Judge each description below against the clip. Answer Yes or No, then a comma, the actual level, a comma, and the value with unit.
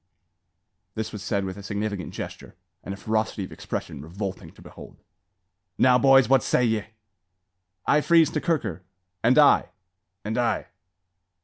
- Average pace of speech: Yes, average, 145 wpm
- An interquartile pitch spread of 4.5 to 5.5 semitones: Yes, average, 4.8 semitones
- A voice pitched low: Yes, low, 110 Hz